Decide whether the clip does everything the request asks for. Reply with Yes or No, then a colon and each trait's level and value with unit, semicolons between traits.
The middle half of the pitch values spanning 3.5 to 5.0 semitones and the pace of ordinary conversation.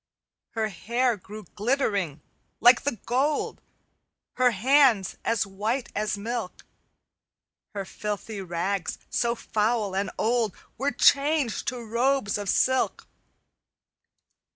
No: average, 3.8 semitones; slow, 105 wpm